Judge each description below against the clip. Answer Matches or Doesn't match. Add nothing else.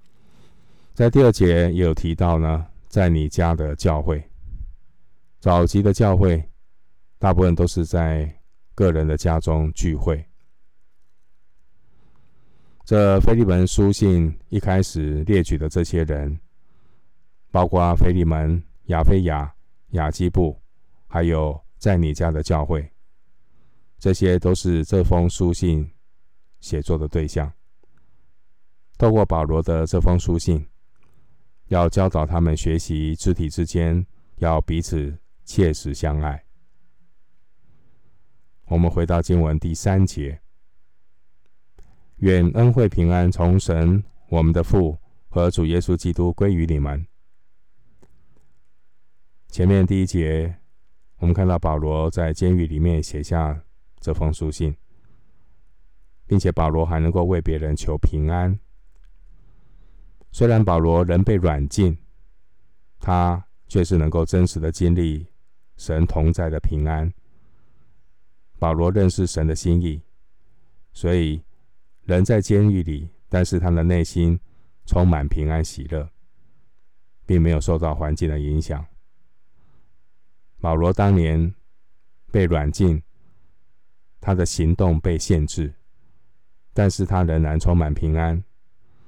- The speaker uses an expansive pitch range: Doesn't match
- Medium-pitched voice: Doesn't match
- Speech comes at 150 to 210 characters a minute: Matches